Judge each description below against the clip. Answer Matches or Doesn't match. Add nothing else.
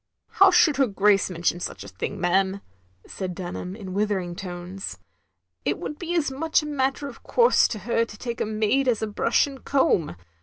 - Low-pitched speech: Doesn't match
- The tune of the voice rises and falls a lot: Matches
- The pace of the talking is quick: Matches